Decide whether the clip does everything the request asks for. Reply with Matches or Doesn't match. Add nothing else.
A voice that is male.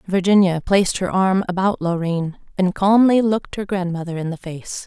Doesn't match